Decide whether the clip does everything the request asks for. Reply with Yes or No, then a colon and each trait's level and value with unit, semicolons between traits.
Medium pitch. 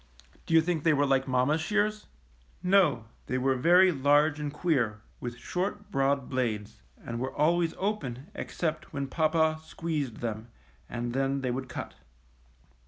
Yes: medium, 145 Hz